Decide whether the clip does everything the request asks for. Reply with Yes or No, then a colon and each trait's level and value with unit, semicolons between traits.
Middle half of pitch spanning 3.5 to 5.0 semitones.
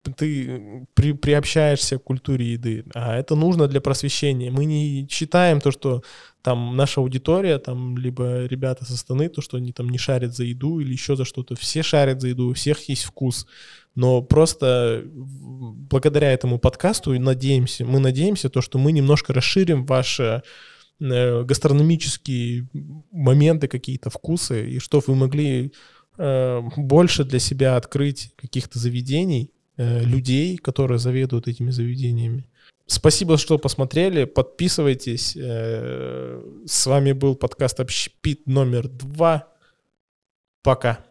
No: average, 2.8 semitones